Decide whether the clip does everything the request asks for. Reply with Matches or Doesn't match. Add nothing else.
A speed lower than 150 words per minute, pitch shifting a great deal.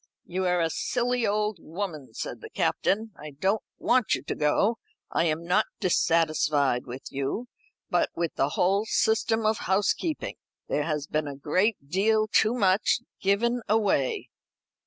Doesn't match